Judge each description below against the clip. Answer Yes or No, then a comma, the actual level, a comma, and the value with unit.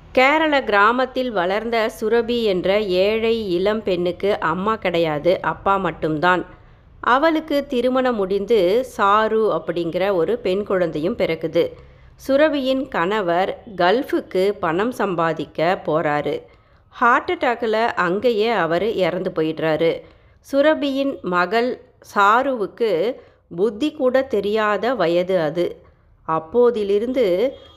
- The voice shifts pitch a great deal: Yes, wide, 6.2 semitones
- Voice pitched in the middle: No, high, 205 Hz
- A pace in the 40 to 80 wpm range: No, average, 90 wpm